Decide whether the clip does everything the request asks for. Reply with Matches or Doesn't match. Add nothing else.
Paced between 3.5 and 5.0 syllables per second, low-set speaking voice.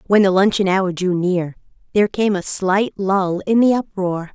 Doesn't match